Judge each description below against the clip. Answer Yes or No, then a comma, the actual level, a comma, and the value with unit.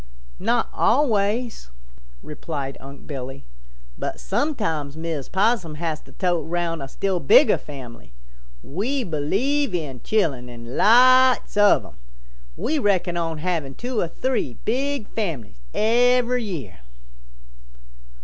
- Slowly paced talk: Yes, slow, 120 wpm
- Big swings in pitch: Yes, wide, 8.5 semitones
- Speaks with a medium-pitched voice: Yes, medium, 175 Hz